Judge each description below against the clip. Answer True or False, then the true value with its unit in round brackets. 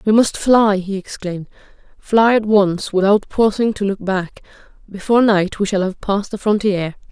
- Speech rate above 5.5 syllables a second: False (4.9 syllables/s)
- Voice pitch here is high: True (200 Hz)